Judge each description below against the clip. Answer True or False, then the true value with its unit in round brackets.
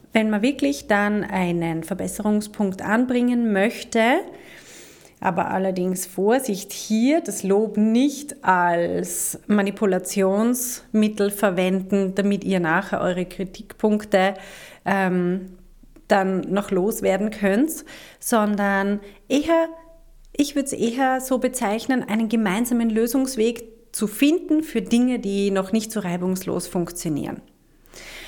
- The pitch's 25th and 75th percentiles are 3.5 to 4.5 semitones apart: True (4.1 semitones)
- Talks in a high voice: True (210 Hz)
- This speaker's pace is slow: True (105 wpm)